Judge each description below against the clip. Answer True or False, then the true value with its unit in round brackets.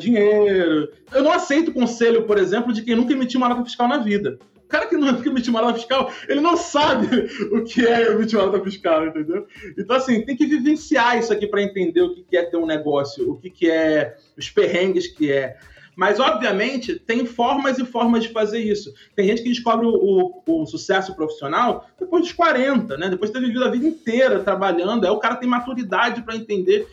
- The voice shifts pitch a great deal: True (6.2 semitones)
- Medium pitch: False (235 Hz)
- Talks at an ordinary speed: False (210 wpm)